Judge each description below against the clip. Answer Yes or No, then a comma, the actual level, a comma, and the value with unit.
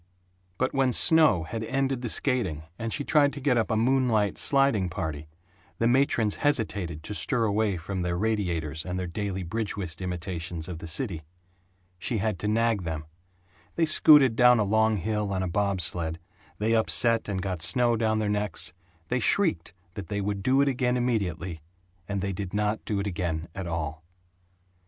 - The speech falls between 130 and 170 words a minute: No, average, 185 wpm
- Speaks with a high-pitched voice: No, low, 105 Hz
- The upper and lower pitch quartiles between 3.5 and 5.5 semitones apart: Yes, average, 4.9 semitones